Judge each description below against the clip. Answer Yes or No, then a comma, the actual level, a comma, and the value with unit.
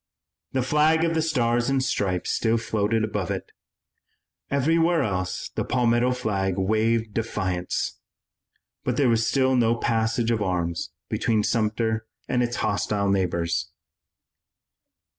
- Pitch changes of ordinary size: Yes, average, 3.6 semitones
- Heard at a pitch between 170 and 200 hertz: No, low, 115 Hz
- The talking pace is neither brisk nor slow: No, slow, 125 wpm